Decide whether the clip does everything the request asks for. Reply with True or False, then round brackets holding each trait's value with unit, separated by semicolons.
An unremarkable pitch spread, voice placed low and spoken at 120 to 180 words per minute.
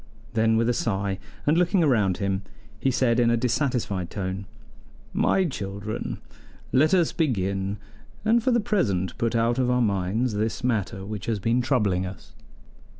True (4.6 semitones; 115 Hz; 160 wpm)